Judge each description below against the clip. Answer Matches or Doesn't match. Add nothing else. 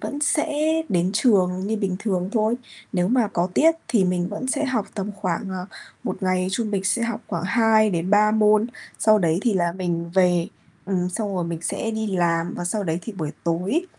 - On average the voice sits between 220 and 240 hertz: Doesn't match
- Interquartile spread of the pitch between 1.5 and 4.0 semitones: Matches